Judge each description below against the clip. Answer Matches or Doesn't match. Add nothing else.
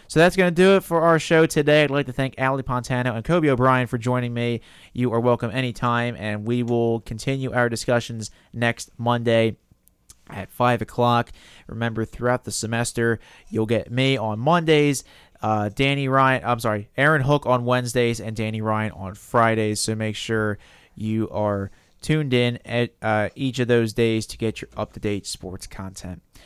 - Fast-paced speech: Doesn't match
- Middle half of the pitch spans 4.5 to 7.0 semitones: Doesn't match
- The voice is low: Matches